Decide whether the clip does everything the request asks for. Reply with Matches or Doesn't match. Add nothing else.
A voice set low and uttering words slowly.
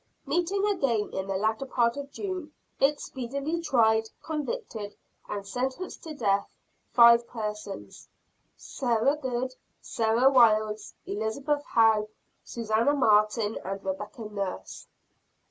Doesn't match